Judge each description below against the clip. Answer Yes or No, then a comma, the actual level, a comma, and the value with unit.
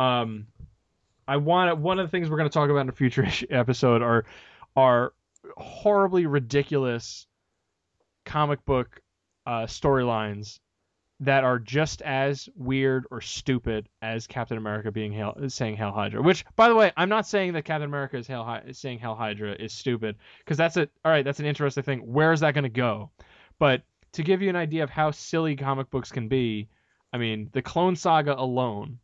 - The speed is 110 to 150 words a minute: No, average, 185 wpm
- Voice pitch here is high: No, low, 130 Hz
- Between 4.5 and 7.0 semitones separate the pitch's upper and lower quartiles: Yes, average, 5.1 semitones